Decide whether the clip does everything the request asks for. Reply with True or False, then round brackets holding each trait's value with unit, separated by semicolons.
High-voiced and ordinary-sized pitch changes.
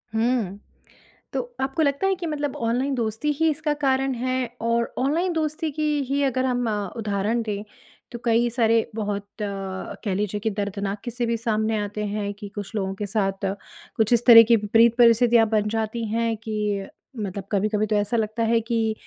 True (225 Hz; 3.0 semitones)